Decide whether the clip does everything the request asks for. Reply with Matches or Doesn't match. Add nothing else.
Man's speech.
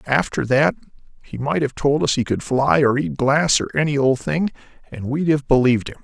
Matches